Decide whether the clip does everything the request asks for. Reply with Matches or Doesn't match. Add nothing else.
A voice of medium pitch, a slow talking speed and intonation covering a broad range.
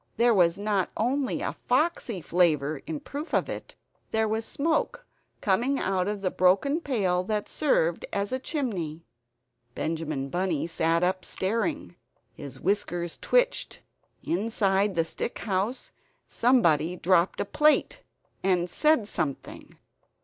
Doesn't match